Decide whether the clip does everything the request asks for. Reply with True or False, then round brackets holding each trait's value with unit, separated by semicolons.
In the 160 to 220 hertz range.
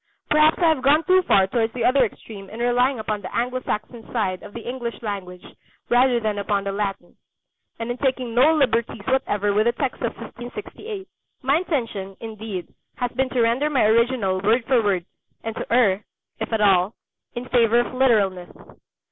False (235 Hz)